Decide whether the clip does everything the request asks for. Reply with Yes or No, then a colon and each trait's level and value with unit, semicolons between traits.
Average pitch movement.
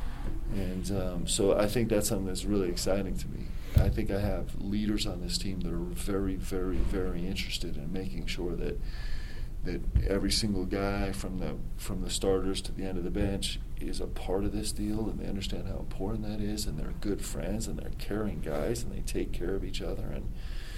No: narrow, 1.9 semitones